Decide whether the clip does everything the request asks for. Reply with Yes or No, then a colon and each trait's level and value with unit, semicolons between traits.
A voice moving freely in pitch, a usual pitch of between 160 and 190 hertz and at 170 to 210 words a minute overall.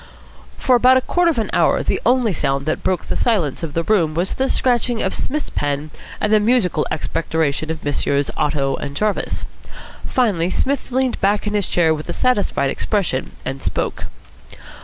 Yes: wide, 7.9 semitones; medium, 185 Hz; average, 180 wpm